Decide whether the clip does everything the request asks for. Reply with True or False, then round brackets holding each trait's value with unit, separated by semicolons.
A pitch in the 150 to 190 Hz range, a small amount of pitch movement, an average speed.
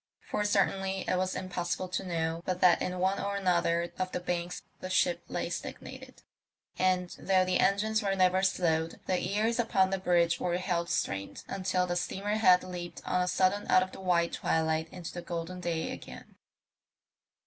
True (185 Hz; 1.7 semitones; 180 wpm)